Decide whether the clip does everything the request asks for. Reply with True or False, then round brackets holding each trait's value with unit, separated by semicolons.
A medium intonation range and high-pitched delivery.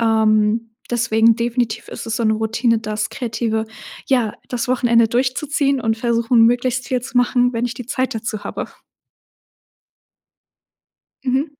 False (1.9 semitones; 235 Hz)